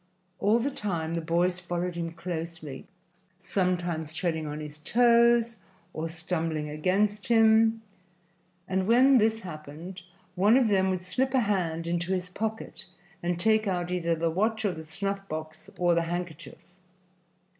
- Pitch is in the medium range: Yes, medium, 180 Hz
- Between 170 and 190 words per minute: No, average, 150 wpm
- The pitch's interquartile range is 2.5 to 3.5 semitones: No, average, 4.2 semitones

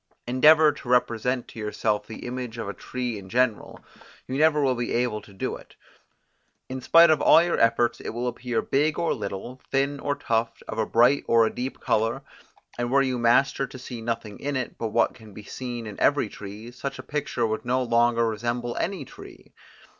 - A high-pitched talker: No, low, 120 Hz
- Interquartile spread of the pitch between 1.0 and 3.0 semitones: Yes, narrow, 2.6 semitones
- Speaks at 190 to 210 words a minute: Yes, fast, 205 wpm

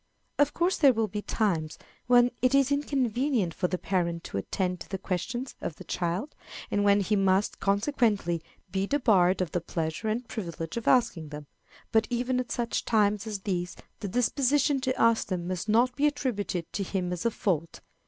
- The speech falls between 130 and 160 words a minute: No, average, 190 wpm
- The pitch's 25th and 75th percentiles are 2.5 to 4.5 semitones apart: No, wide, 5.5 semitones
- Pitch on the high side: Yes, high, 205 Hz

